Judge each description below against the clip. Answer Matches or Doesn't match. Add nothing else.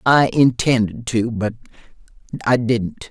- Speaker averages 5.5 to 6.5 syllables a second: Doesn't match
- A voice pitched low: Matches